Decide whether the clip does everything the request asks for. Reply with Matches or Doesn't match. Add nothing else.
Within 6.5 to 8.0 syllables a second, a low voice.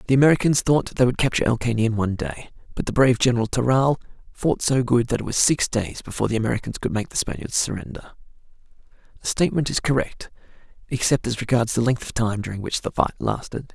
Matches